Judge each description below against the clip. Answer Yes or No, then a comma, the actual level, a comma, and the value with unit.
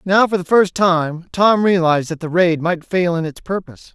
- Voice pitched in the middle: Yes, medium, 175 Hz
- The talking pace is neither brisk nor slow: No, fast, 230 wpm